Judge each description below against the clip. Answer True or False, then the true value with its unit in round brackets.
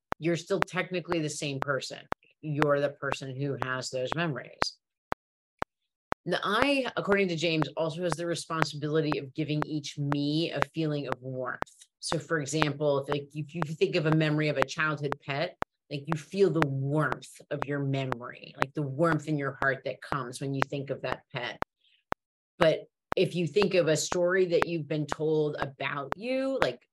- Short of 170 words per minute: False (180 wpm)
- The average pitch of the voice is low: False (150 Hz)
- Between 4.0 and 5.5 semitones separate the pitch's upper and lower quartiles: False (2.9 semitones)